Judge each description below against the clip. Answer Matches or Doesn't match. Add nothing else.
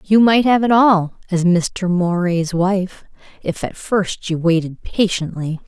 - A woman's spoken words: Matches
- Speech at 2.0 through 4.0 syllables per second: Matches